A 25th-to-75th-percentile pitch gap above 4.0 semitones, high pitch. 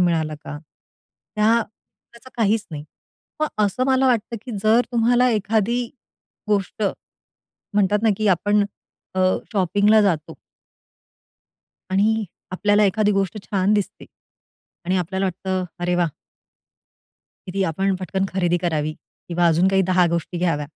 No: average, 3.3 semitones; high, 195 Hz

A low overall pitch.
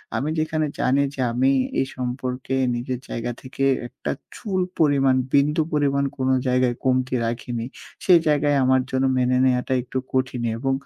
Yes: low, 130 Hz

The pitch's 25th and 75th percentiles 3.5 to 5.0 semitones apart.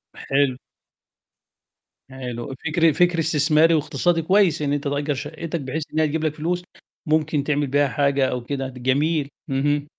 No: narrow, 2.5 semitones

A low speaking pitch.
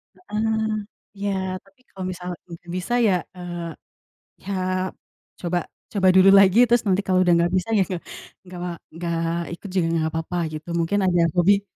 No: medium, 185 Hz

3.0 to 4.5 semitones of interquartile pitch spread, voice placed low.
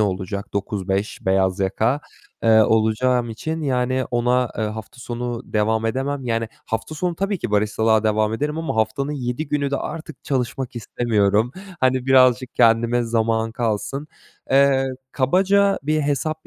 Yes: average, 3.8 semitones; low, 120 Hz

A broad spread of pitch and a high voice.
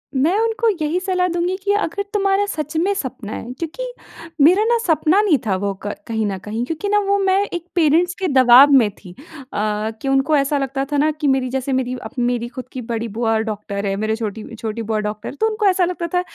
Yes: wide, 8.3 semitones; very high, 275 Hz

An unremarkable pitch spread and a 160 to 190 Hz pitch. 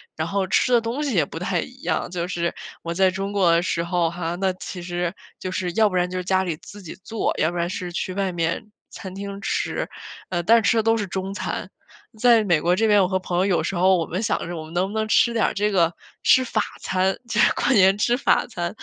Yes: average, 3.1 semitones; medium, 185 Hz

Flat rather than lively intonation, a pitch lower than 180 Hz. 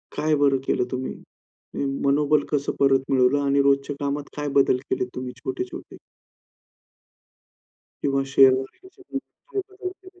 Yes: narrow, 2.2 semitones; medium, 140 Hz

